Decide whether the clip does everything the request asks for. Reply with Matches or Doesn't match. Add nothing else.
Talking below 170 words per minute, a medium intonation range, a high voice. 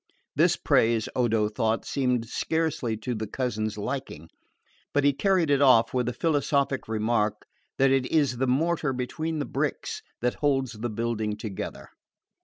Doesn't match